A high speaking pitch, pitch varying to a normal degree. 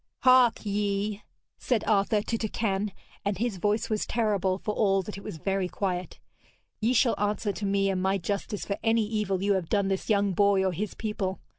No: high, 200 Hz; narrow, 1.7 semitones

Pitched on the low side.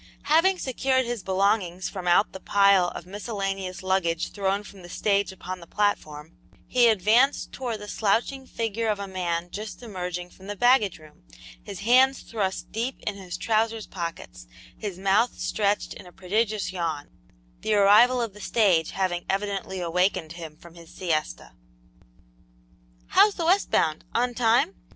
No: high, 200 Hz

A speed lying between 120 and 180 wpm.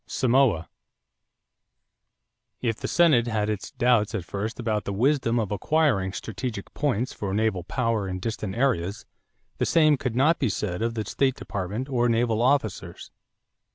Yes: average, 155 wpm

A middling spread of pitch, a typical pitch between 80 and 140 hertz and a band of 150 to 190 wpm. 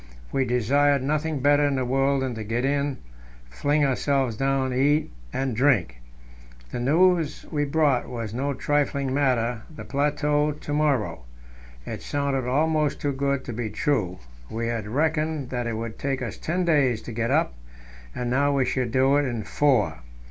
Yes: average, 3.1 semitones; low, 135 Hz; average, 170 wpm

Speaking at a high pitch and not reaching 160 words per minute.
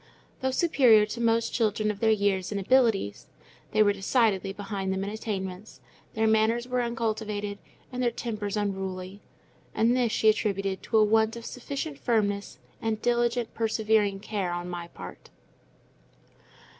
Yes: high, 215 Hz; average, 150 wpm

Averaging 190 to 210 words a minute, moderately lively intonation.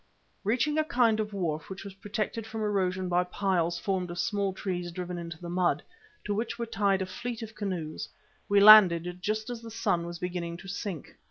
Yes: average, 200 wpm; average, 3.4 semitones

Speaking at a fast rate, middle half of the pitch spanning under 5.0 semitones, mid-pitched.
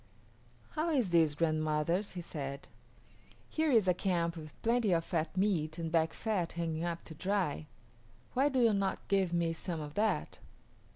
No: average, 170 wpm; average, 4.1 semitones; medium, 170 Hz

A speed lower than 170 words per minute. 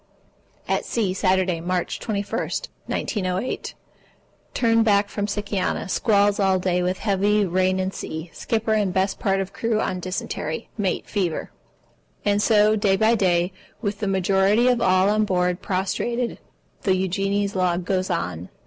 Yes: average, 150 wpm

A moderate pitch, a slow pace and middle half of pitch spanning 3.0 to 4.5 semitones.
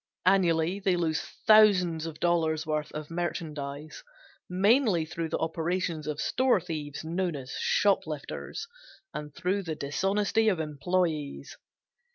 Yes: medium, 165 Hz; slow, 125 wpm; average, 3.3 semitones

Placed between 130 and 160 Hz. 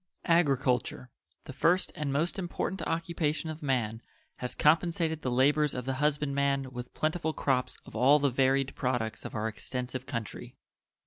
Yes: medium, 140 Hz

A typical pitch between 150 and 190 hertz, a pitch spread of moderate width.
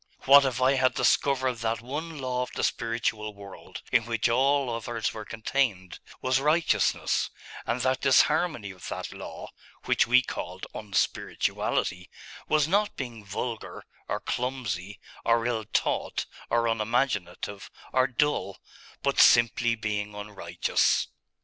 No: low, 120 Hz; average, 3.6 semitones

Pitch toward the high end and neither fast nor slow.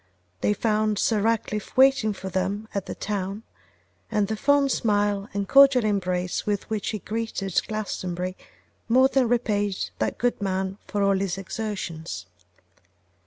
Yes: high, 205 Hz; average, 145 wpm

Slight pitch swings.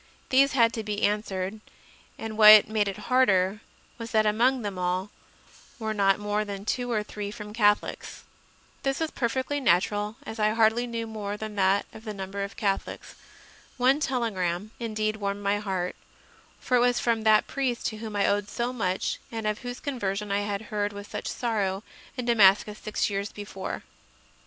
Yes: narrow, 2.3 semitones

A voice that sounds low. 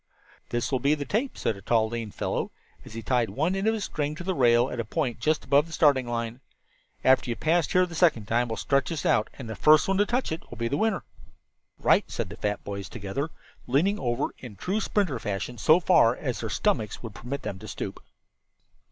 Yes: low, 130 Hz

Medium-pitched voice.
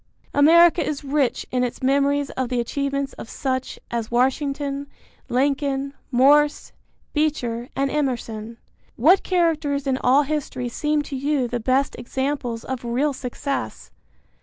No: very high, 275 Hz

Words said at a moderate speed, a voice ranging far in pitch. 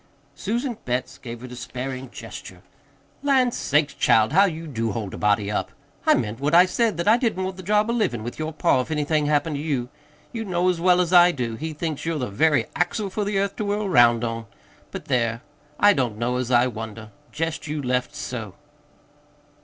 No: fast, 215 wpm; wide, 7.2 semitones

